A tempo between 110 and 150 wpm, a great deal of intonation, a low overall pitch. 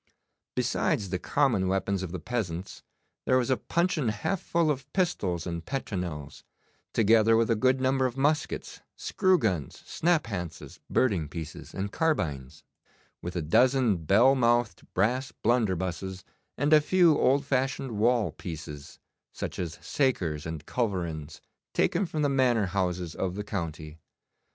Yes: average, 140 wpm; wide, 7.1 semitones; low, 110 Hz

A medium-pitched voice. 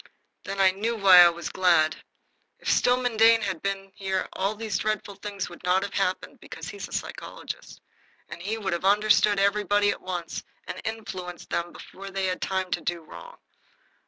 No: high, 195 Hz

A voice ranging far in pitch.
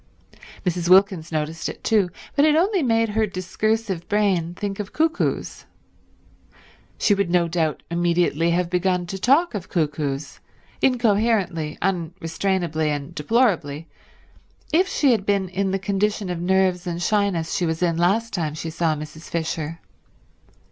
No: average, 4.0 semitones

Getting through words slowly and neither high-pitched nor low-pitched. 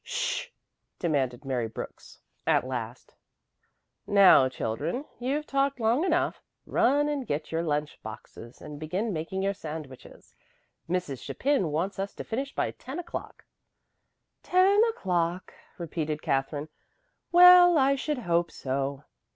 Yes: slow, 130 wpm; medium, 180 Hz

